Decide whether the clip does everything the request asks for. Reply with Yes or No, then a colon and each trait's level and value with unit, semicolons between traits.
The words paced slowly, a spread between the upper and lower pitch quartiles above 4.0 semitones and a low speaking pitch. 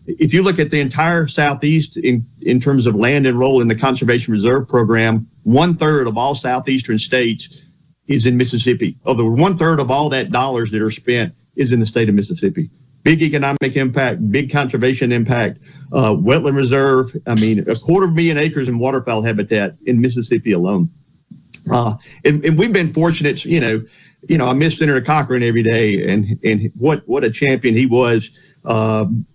No: average, 185 wpm; average, 4.5 semitones; low, 130 Hz